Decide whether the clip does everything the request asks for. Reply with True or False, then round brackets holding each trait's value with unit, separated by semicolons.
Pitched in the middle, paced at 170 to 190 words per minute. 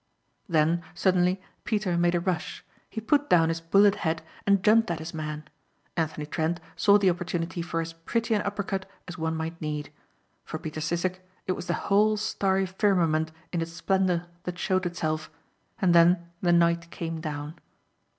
True (175 Hz; 175 wpm)